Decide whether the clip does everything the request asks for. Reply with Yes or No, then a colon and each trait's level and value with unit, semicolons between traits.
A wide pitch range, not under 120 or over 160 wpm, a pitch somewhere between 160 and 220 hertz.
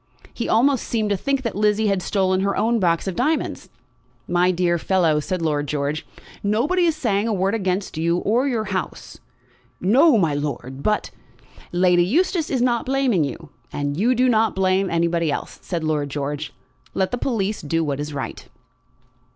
No: wide, 5.8 semitones; average, 180 wpm; high, 190 Hz